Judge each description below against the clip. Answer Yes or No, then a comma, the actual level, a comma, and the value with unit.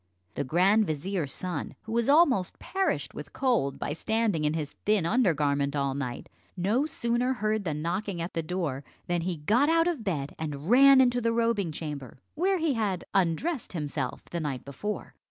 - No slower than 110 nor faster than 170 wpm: No, average, 185 wpm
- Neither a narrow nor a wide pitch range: No, wide, 7.6 semitones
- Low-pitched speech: No, medium, 185 Hz